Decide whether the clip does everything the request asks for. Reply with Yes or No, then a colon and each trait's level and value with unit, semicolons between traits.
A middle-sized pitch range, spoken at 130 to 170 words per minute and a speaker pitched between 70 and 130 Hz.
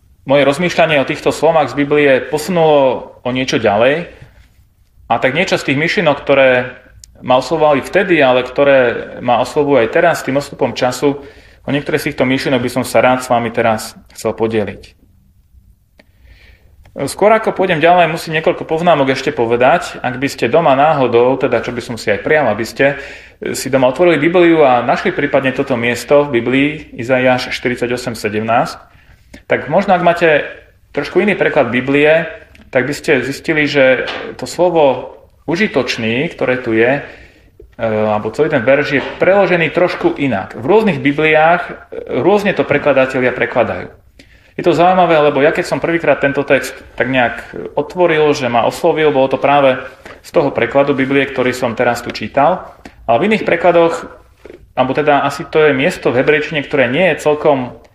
No: average, 4.1 semitones; fast, 165 wpm; medium, 140 Hz